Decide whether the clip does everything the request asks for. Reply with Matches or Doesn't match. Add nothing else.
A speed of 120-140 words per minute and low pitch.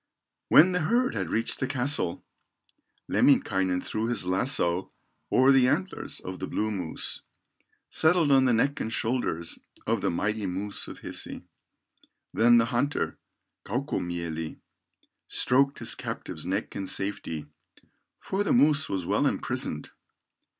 Matches